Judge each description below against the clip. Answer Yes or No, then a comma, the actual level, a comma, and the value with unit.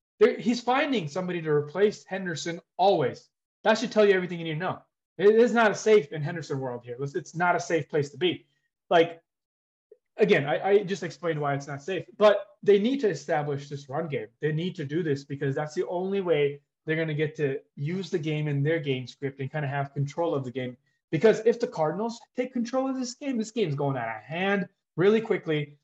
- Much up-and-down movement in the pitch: Yes, wide, 6.0 semitones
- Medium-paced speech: No, fast, 225 wpm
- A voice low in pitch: No, medium, 170 Hz